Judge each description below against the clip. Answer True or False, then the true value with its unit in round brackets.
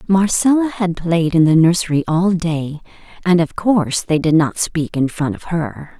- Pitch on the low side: False (170 Hz)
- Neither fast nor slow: True (190 wpm)